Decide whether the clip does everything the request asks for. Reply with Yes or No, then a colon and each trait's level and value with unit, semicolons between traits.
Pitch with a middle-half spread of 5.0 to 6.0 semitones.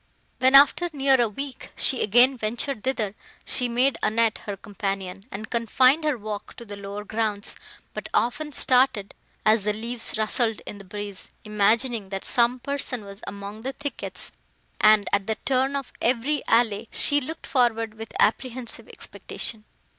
No: average, 3.8 semitones